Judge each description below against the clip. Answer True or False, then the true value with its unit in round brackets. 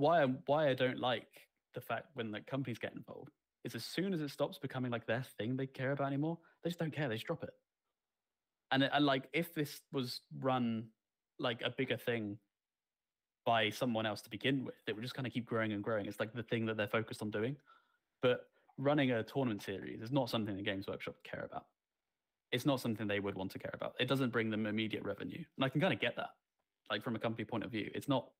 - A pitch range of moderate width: True (4.0 semitones)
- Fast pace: True (245 wpm)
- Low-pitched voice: True (125 Hz)